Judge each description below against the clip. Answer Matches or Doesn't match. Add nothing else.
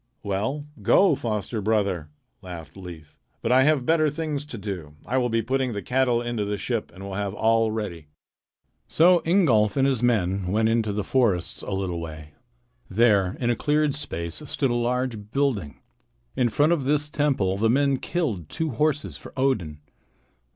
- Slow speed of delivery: Doesn't match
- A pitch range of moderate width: Doesn't match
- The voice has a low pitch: Matches